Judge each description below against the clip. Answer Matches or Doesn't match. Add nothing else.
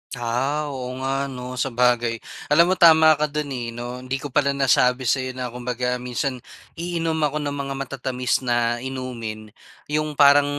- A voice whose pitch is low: Matches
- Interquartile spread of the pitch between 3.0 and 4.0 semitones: Doesn't match